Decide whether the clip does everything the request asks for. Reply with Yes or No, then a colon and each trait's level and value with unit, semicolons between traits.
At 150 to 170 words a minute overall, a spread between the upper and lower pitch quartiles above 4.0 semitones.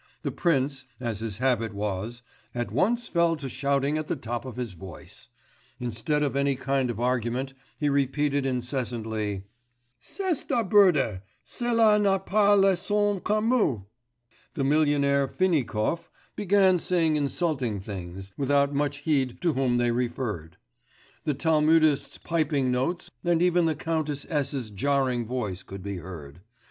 No: average, 140 wpm; wide, 5.5 semitones